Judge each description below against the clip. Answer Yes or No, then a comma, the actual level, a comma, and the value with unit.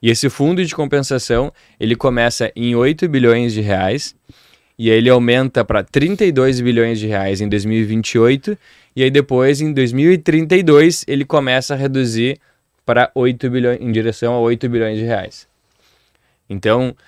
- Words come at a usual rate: Yes, average, 150 wpm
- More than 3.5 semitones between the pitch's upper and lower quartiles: No, average, 3.2 semitones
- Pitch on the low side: Yes, low, 125 Hz